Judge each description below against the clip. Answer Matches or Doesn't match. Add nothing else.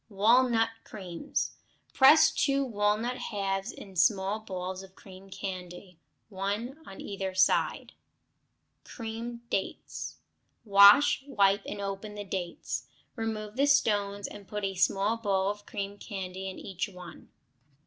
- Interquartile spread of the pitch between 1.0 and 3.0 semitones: Matches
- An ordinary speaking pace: Doesn't match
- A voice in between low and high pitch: Doesn't match